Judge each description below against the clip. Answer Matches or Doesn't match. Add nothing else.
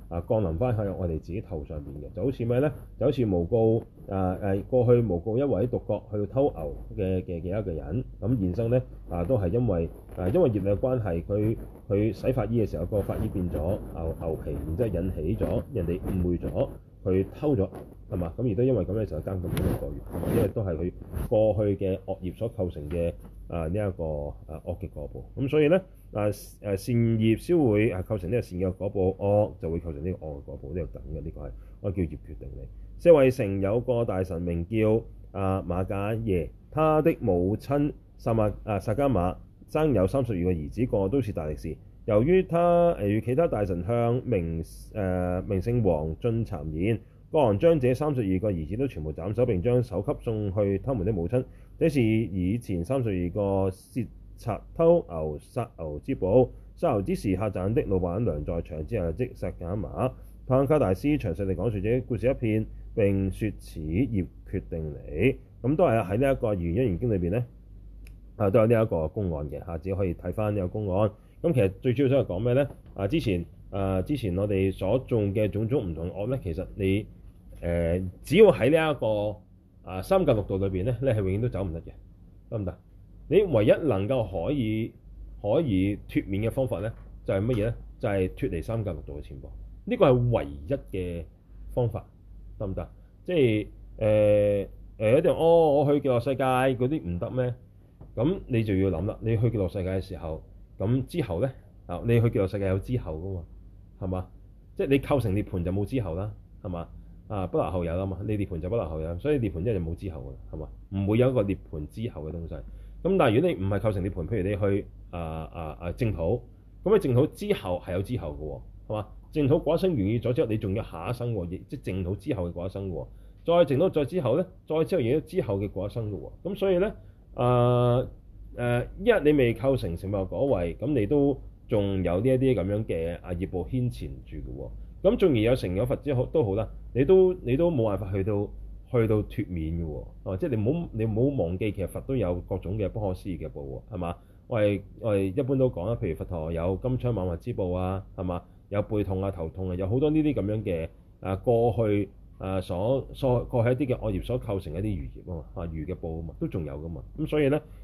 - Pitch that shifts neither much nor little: Matches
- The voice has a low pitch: Matches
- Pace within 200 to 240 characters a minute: Doesn't match